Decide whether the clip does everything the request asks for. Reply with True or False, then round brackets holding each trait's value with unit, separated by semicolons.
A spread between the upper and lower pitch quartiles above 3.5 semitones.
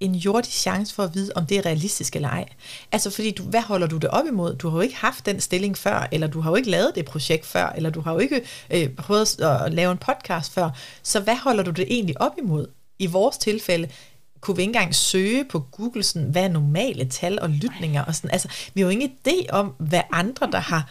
True (4.2 semitones)